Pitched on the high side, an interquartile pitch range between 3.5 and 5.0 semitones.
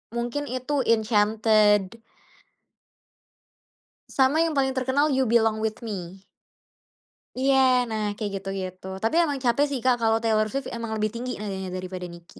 Yes: high, 225 Hz; average, 3.9 semitones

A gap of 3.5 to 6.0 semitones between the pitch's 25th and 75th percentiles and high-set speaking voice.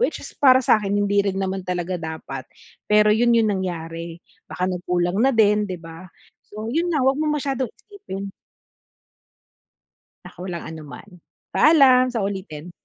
Yes: average, 5.2 semitones; high, 200 Hz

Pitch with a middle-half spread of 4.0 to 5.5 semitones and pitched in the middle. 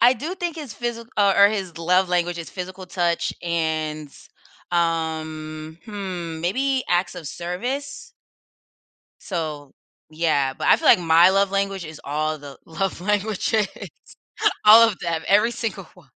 Yes: average, 4.5 semitones; medium, 180 Hz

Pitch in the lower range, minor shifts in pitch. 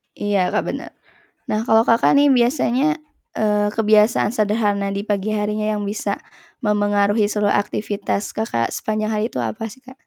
No: high, 210 Hz; narrow, 1.4 semitones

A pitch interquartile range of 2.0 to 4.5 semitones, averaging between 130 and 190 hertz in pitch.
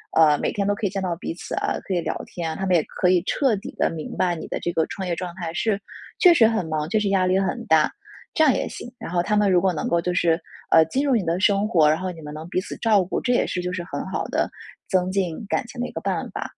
Yes: average, 3.4 semitones; medium, 185 Hz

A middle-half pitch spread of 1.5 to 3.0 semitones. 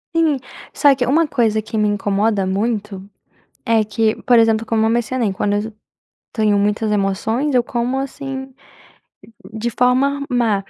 No: average, 3.4 semitones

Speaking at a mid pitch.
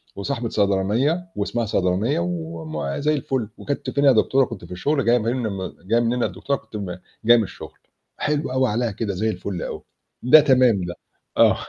No: low, 115 Hz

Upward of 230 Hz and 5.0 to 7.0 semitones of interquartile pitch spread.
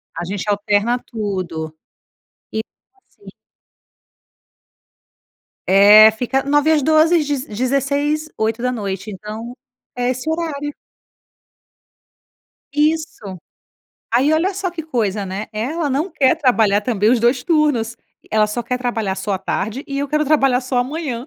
Yes: very high, 250 Hz; wide, 5.6 semitones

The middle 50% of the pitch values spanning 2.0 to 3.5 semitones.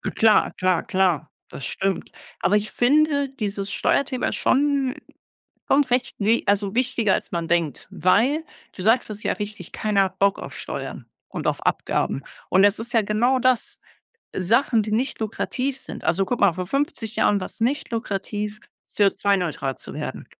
No: average, 4.4 semitones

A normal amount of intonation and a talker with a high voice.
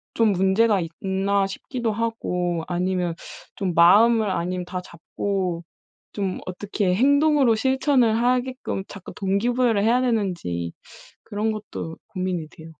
Yes: average, 4.2 semitones; high, 200 Hz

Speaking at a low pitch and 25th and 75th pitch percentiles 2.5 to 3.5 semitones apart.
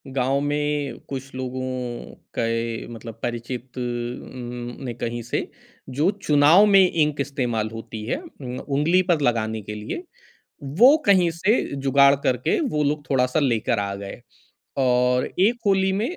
No: low, 130 Hz; average, 3.9 semitones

